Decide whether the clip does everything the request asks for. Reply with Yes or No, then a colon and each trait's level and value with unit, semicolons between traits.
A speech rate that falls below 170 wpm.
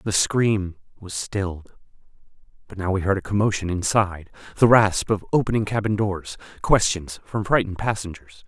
Yes: average, 140 wpm